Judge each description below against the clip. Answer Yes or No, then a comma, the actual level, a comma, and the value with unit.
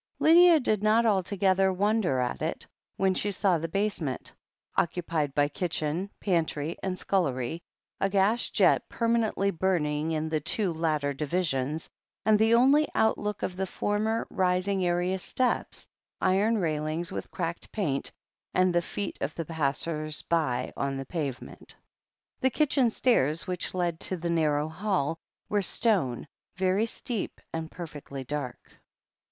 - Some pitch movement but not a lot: Yes, average, 4.9 semitones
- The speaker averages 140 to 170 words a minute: Yes, average, 145 wpm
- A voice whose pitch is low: No, medium, 180 Hz